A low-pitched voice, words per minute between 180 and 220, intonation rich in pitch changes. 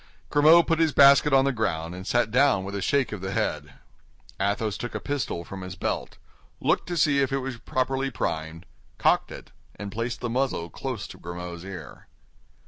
Yes: low, 115 Hz; average, 195 wpm; wide, 6.4 semitones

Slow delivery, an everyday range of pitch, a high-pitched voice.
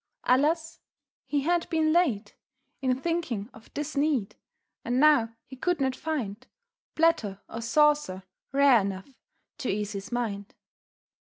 No: slow, 130 wpm; wide, 6.1 semitones; very high, 260 Hz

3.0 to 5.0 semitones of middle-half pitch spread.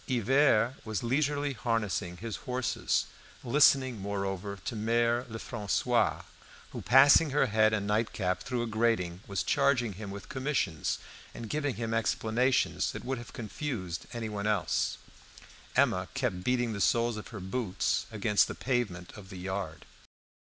Yes: average, 3.9 semitones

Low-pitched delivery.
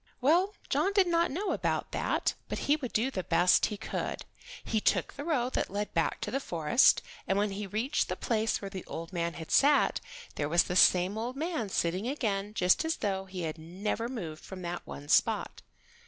No: high, 205 Hz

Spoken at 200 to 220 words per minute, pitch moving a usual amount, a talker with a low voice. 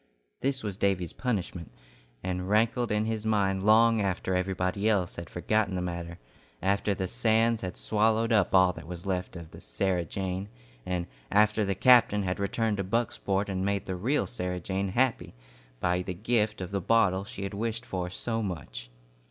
No: average, 180 wpm; average, 3.1 semitones; low, 100 Hz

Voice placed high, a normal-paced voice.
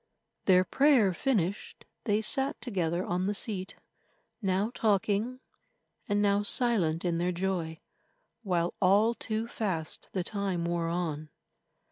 No: high, 195 Hz; slow, 125 wpm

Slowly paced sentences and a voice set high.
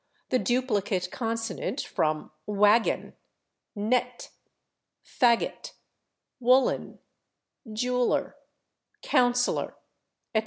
Yes: slow, 65 wpm; high, 235 Hz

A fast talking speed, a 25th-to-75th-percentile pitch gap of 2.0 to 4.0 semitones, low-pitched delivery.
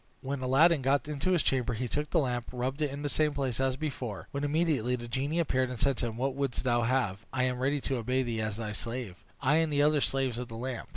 Yes: fast, 270 wpm; average, 2.9 semitones; low, 130 Hz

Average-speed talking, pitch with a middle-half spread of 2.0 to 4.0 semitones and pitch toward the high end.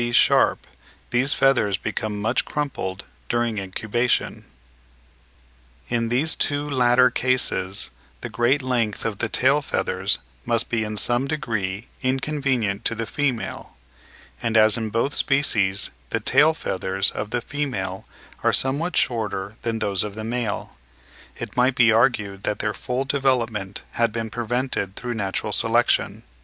No: average, 145 wpm; average, 3.6 semitones; low, 120 Hz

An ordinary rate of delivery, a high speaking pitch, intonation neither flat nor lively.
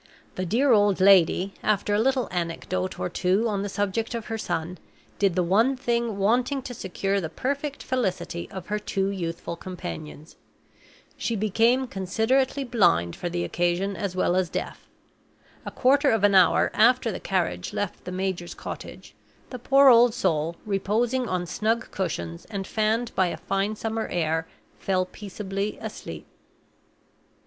Yes: average, 155 wpm; high, 200 Hz; average, 4.1 semitones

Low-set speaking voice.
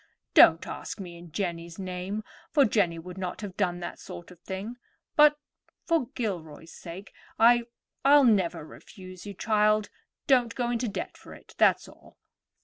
No: high, 195 Hz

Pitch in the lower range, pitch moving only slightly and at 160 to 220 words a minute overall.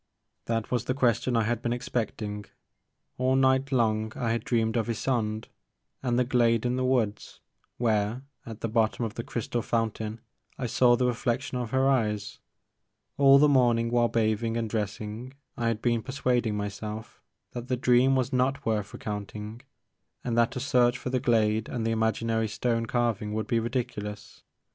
Yes: low, 115 Hz; narrow, 2.2 semitones; average, 180 wpm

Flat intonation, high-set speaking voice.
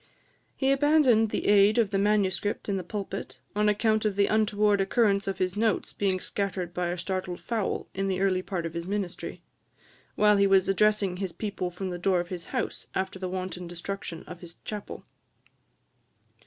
Yes: narrow, 2.3 semitones; high, 195 Hz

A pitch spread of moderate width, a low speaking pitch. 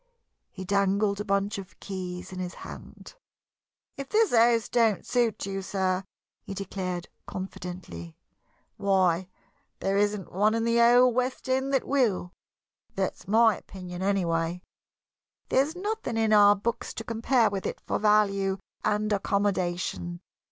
No: average, 3.4 semitones; high, 200 Hz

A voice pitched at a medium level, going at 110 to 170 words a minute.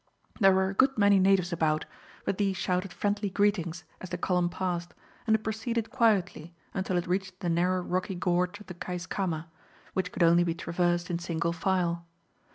No: medium, 180 Hz; average, 180 wpm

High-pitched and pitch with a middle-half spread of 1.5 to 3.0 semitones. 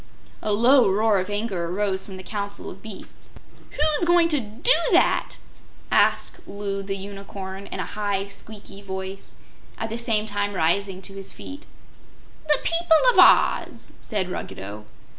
Yes: high, 200 Hz; average, 2.7 semitones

